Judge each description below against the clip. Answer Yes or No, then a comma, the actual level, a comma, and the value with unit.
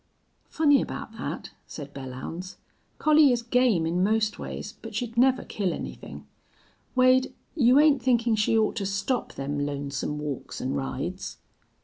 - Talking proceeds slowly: No, average, 145 wpm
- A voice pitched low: No, high, 220 Hz